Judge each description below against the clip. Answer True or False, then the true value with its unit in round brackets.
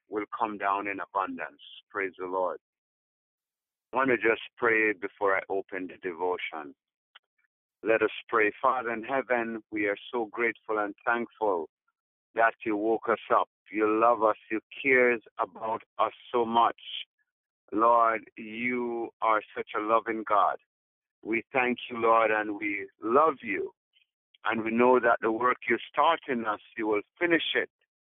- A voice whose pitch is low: True (115 Hz)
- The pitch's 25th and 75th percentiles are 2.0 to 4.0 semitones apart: True (2.8 semitones)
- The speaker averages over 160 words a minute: False (155 wpm)